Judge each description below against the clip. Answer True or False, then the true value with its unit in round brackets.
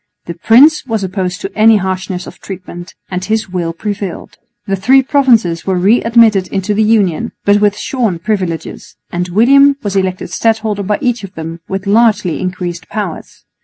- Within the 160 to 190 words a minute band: True (170 wpm)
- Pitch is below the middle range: False (200 Hz)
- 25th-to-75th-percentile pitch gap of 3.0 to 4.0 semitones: True (3.5 semitones)